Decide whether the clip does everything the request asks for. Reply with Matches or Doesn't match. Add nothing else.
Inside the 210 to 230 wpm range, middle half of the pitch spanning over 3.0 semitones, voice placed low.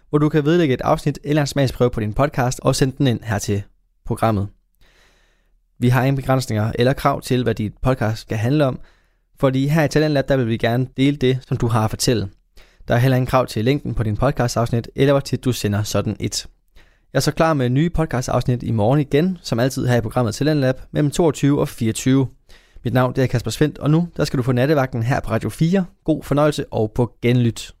Matches